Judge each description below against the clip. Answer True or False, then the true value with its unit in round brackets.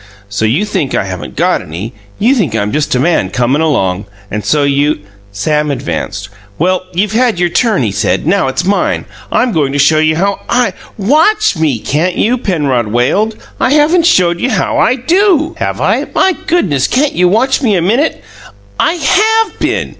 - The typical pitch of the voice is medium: True (175 Hz)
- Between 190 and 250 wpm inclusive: True (195 wpm)